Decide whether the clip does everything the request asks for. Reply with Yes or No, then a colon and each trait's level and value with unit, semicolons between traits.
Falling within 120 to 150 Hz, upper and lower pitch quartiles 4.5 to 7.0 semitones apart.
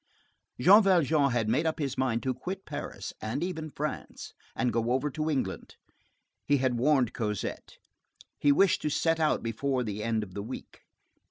Yes: low, 135 Hz; average, 5.0 semitones